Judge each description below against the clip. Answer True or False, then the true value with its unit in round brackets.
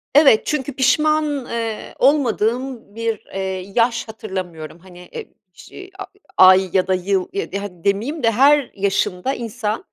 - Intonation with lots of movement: True (5.9 semitones)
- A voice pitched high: True (225 Hz)